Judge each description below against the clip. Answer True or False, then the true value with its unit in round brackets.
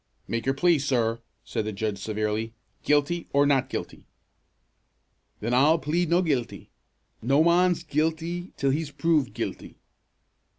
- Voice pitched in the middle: True (145 Hz)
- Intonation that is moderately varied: False (6.0 semitones)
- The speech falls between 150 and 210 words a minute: False (135 wpm)